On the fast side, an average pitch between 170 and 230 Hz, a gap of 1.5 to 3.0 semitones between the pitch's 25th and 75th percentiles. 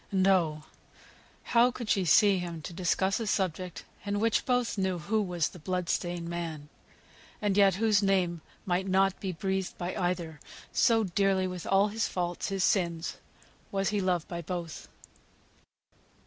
No: average, 160 wpm; medium, 185 Hz; narrow, 2.5 semitones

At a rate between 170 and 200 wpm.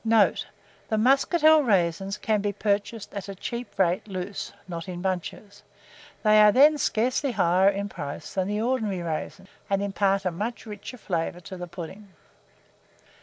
No: average, 160 wpm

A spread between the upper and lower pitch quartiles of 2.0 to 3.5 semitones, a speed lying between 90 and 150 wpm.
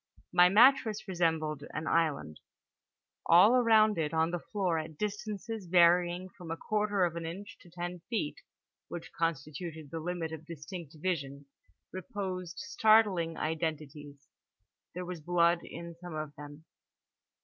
Yes: average, 2.8 semitones; average, 140 wpm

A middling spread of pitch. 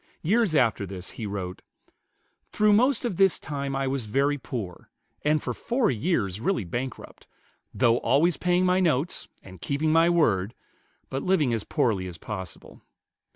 No: wide, 8.3 semitones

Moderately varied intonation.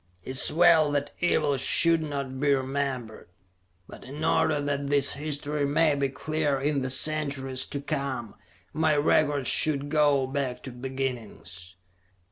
No: narrow, 2.2 semitones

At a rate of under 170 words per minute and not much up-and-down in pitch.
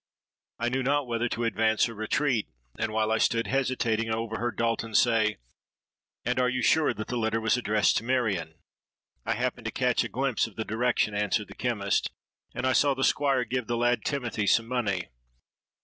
No: average, 190 wpm; narrow, 2.2 semitones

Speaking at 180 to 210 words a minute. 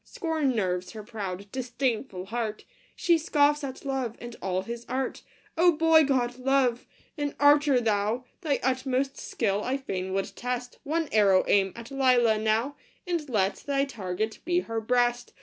No: average, 160 wpm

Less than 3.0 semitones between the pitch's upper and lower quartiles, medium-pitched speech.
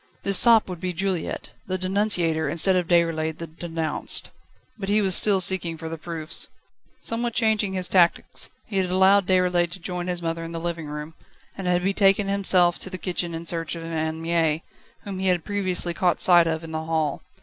Yes: narrow, 2.5 semitones; medium, 175 Hz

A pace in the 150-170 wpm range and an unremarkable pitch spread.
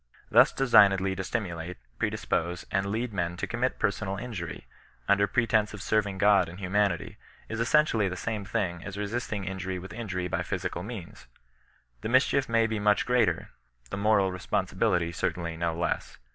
Yes: average, 165 wpm; average, 3.5 semitones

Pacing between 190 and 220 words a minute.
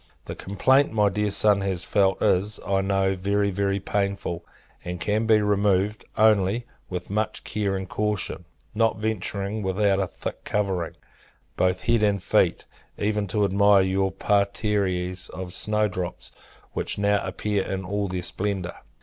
No: average, 150 wpm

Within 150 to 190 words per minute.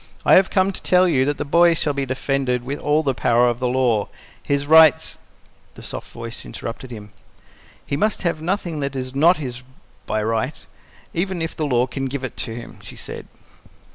No: fast, 205 wpm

